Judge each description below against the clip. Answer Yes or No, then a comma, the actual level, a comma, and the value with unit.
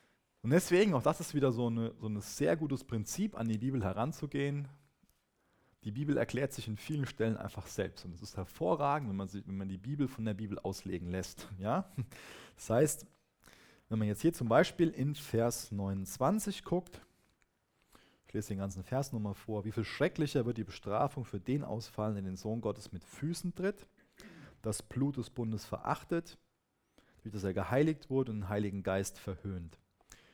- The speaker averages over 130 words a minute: Yes, average, 180 wpm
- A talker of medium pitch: No, low, 115 Hz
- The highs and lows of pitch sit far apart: Yes, wide, 6.0 semitones